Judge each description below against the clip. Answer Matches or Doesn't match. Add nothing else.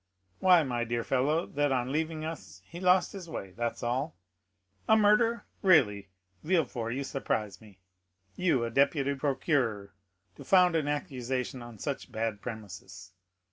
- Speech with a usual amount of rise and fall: Doesn't match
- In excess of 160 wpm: Doesn't match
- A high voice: Doesn't match